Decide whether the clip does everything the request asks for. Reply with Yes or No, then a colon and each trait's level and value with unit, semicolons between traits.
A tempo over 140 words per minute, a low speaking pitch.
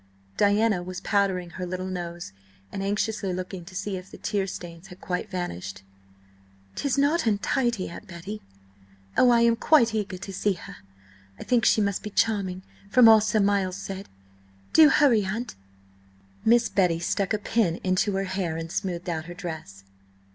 No: average, 170 wpm; high, 195 Hz